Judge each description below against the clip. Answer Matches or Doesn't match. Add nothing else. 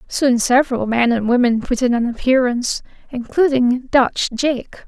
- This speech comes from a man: Doesn't match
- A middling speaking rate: Matches